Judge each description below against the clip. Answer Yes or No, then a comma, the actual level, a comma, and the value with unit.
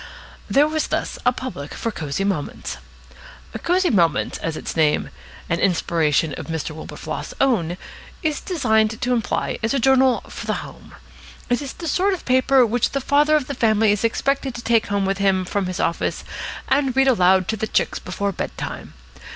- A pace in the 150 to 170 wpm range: No, average, 185 wpm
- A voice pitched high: Yes, high, 225 Hz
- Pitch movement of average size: No, wide, 6.4 semitones